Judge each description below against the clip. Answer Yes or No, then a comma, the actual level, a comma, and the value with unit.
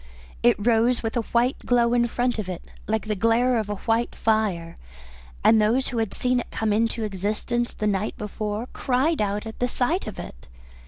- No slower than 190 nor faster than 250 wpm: Yes, average, 200 wpm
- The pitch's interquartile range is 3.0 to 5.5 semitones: No, narrow, 2.4 semitones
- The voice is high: Yes, high, 225 Hz